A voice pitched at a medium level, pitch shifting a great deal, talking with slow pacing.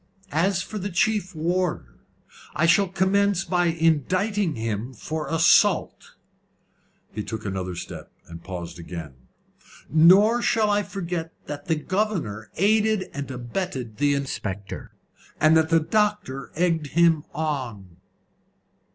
Yes: medium, 160 Hz; wide, 7.4 semitones; slow, 125 wpm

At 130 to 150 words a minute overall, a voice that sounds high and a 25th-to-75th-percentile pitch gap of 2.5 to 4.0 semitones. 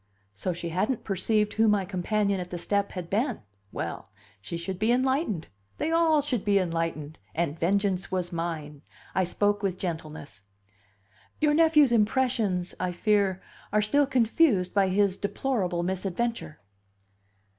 No: average, 145 wpm; high, 195 Hz; average, 4.4 semitones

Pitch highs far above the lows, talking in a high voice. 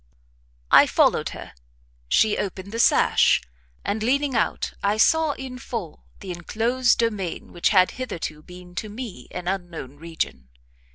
No: average, 5.0 semitones; high, 200 Hz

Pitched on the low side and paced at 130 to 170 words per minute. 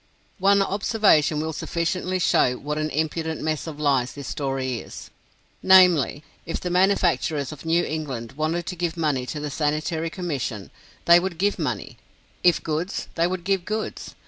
No: medium, 160 Hz; average, 165 wpm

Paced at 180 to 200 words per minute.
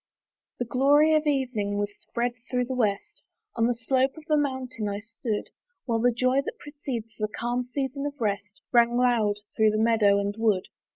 Yes: average, 185 wpm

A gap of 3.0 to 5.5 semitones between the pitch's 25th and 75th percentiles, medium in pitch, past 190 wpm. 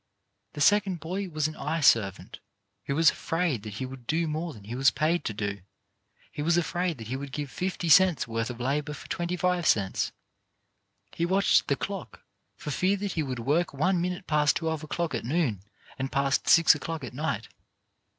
Yes: average, 4.7 semitones; medium, 155 Hz; average, 200 wpm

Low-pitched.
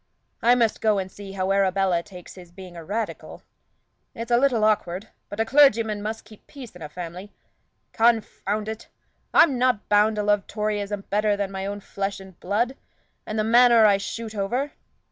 No: high, 210 Hz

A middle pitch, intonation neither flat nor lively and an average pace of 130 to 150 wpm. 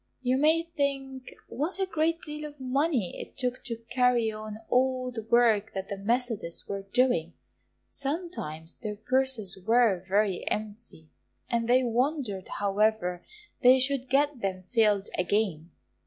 No: high, 240 Hz; average, 4.7 semitones; average, 140 wpm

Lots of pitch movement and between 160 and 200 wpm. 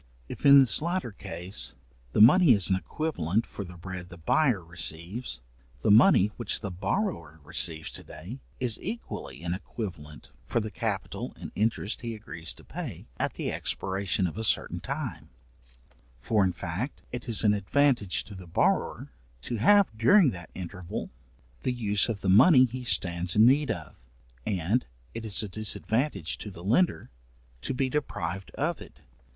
Yes: wide, 5.8 semitones; average, 170 wpm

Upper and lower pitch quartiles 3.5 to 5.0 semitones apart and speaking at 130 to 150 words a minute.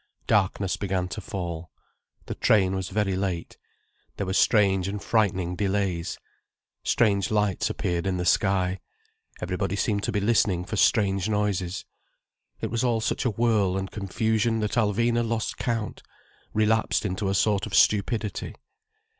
No: narrow, 2.5 semitones; average, 145 wpm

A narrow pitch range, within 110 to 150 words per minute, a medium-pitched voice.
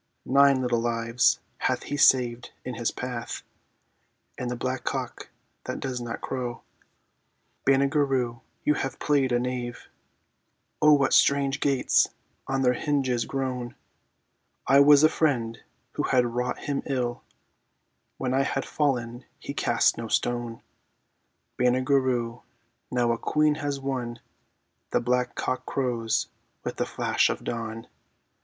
No: narrow, 2.3 semitones; average, 140 wpm; low, 125 Hz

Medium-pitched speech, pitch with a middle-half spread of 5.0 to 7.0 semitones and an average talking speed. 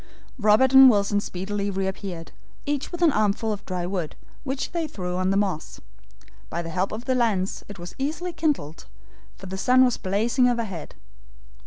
No: high, 205 Hz; wide, 5.4 semitones; average, 175 wpm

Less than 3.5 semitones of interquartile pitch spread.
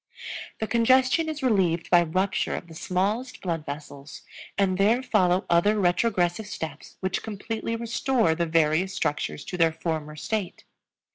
No: average, 5.1 semitones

